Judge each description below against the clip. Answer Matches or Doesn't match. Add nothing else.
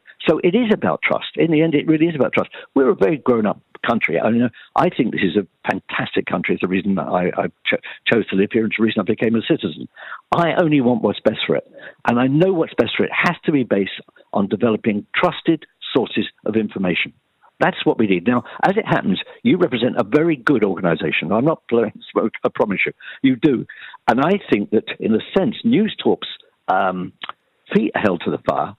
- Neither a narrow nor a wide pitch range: Doesn't match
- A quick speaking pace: Matches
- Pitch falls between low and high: Doesn't match